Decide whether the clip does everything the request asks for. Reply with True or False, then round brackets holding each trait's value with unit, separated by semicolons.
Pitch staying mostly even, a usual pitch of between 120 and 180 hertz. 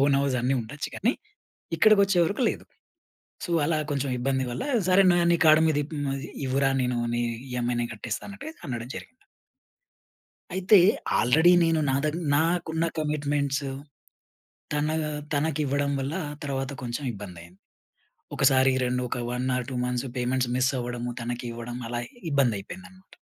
False (4.2 semitones; 140 Hz)